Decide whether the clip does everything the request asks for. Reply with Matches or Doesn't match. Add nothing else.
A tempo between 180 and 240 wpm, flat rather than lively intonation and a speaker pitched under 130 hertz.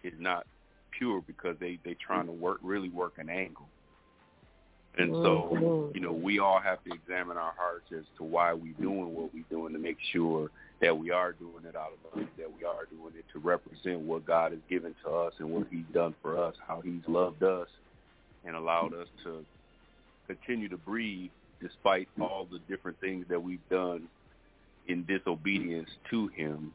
Matches